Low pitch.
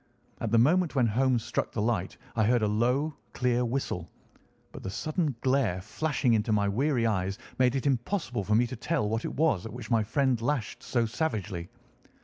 Yes: low, 120 Hz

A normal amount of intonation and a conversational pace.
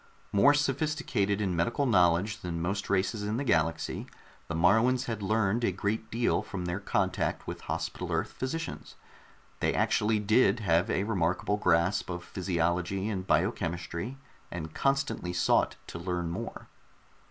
Yes: average, 4.2 semitones; average, 145 wpm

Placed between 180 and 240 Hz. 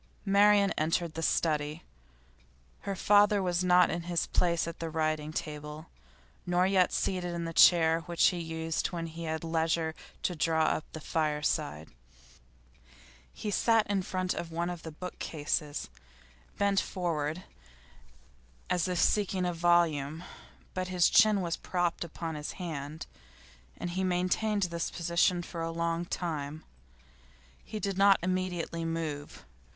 No: medium, 170 Hz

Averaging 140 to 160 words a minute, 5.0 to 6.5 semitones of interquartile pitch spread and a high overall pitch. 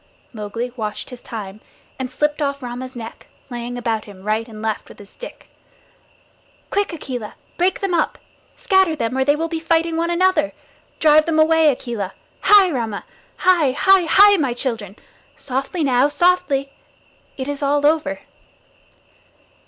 Yes: average, 150 wpm; wide, 5.5 semitones; very high, 280 Hz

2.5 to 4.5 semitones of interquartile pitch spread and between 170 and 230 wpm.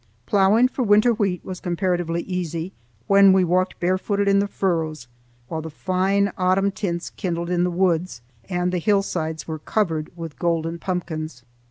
No: average, 2.8 semitones; average, 160 wpm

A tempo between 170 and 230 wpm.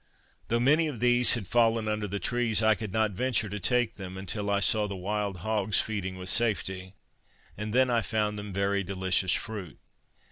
Yes: average, 190 wpm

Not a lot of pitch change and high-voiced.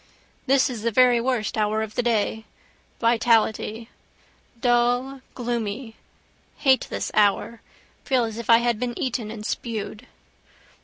Yes: narrow, 2.1 semitones; high, 235 Hz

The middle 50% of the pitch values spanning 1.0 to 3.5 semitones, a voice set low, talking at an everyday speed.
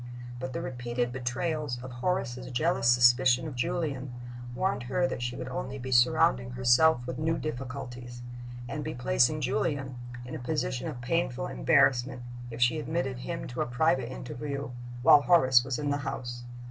Yes: average, 3.0 semitones; low, 130 Hz; average, 165 wpm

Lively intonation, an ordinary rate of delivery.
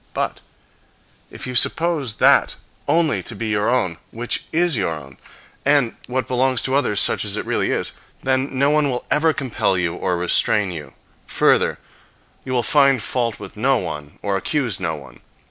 Yes: wide, 6.2 semitones; average, 180 wpm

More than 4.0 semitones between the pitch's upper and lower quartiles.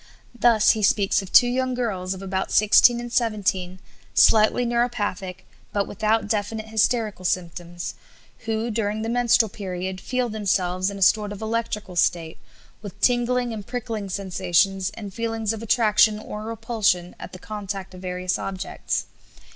No: average, 3.3 semitones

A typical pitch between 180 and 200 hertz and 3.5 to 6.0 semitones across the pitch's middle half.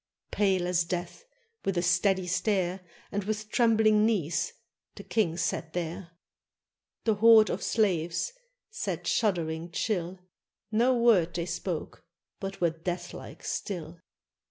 Yes: medium, 185 Hz; average, 3.8 semitones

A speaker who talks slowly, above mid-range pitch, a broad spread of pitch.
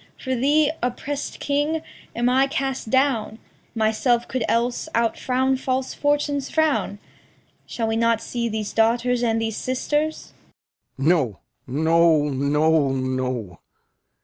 Yes: slow, 120 wpm; high, 235 Hz; wide, 7.9 semitones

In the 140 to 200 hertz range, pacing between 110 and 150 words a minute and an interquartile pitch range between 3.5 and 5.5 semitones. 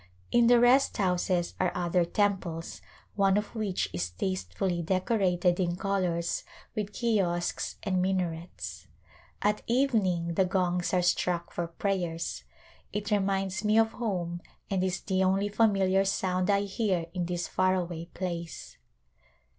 No: medium, 185 Hz; average, 140 wpm; narrow, 2.5 semitones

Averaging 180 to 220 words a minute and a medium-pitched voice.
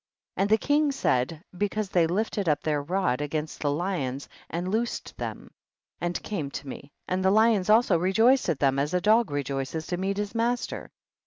Yes: average, 185 wpm; medium, 180 Hz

